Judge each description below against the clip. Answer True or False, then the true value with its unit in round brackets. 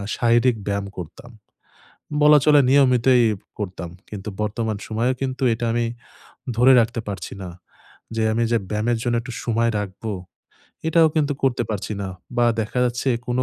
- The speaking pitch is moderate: False (120 Hz)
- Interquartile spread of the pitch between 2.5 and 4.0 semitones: True (3.0 semitones)